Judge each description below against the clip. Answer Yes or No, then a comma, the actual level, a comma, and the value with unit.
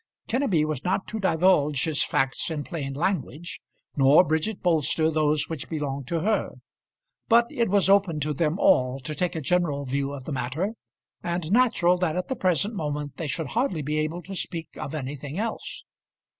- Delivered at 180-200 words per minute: Yes, average, 185 wpm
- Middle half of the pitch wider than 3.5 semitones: Yes, average, 4.1 semitones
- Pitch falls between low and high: Yes, medium, 160 Hz